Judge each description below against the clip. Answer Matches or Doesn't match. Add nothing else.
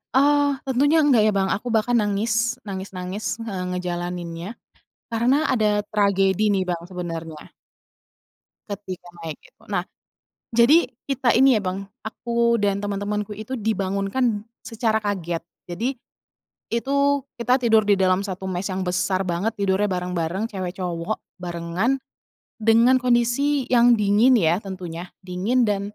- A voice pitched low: Doesn't match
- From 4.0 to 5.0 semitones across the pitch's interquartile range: Matches